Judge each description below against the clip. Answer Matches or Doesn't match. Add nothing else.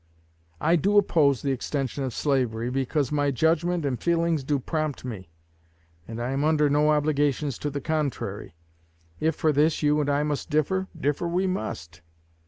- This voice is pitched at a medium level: Matches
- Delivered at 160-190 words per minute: Matches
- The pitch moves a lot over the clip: Doesn't match